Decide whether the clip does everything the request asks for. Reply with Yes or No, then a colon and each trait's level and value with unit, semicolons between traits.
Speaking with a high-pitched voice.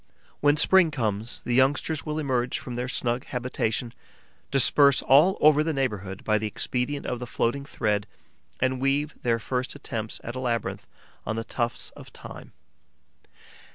No: low, 125 Hz